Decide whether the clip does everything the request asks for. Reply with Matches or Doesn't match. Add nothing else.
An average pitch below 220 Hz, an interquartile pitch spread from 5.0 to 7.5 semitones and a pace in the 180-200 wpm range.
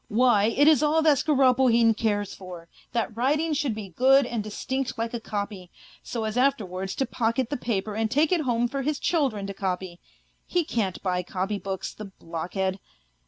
Doesn't match